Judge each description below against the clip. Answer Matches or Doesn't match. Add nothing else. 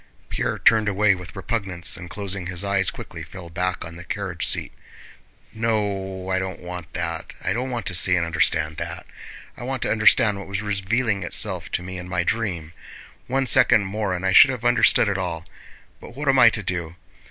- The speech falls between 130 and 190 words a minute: Doesn't match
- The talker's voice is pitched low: Matches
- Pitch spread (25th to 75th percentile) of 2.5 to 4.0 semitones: Matches